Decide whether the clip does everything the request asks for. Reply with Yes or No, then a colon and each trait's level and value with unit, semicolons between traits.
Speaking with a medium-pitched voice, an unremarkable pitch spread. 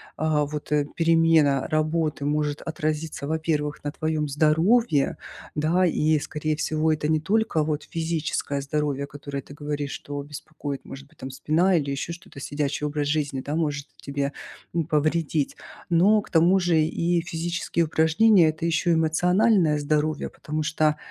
No: medium, 155 Hz; narrow, 2.0 semitones